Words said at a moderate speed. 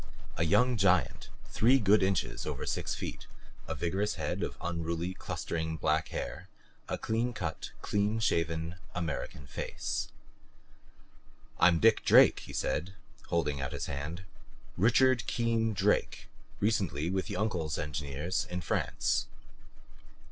No: slow, 125 wpm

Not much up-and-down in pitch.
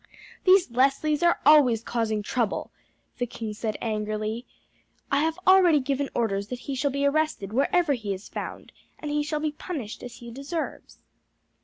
No: average, 5.1 semitones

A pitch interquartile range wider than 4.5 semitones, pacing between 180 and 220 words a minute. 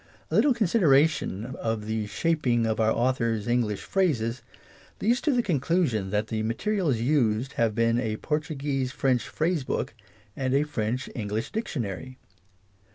No: wide, 5.5 semitones; average, 160 wpm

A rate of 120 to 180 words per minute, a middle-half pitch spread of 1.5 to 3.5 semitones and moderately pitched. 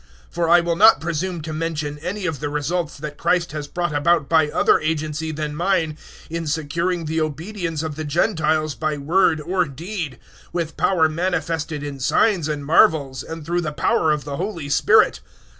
No: average, 190 wpm; narrow, 2.5 semitones; medium, 160 Hz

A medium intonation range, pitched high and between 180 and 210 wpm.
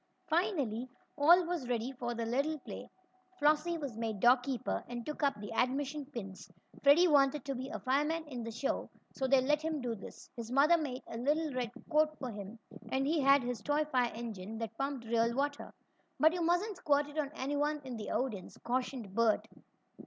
Yes: average, 4.0 semitones; very high, 270 Hz; average, 195 wpm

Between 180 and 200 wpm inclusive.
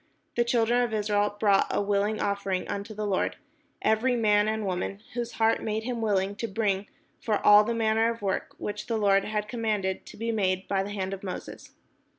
Yes: average, 195 wpm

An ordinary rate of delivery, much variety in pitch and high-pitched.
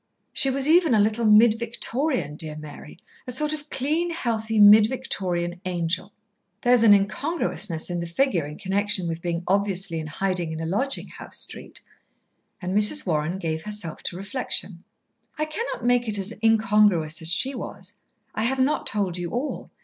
Yes: average, 170 wpm; wide, 6.1 semitones; high, 205 Hz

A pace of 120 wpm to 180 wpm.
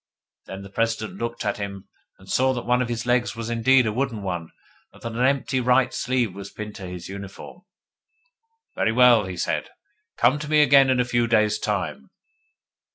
No: average, 195 wpm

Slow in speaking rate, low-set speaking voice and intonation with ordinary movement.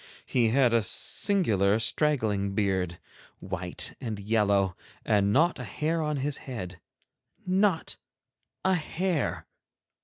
No: slow, 110 wpm; low, 115 Hz; wide, 7.4 semitones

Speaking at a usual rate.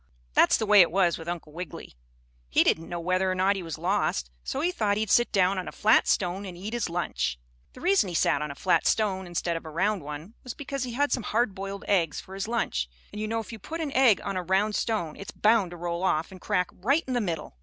No: fast, 265 wpm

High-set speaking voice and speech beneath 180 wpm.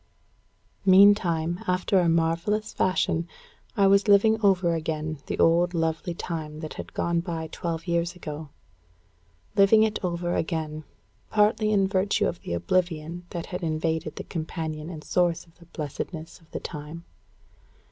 No: medium, 170 Hz; average, 145 wpm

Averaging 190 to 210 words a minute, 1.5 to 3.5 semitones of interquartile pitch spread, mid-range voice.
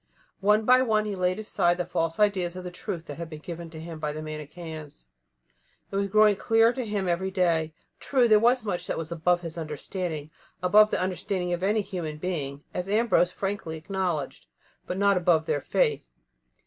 No: average, 195 wpm; average, 4.1 semitones; medium, 180 Hz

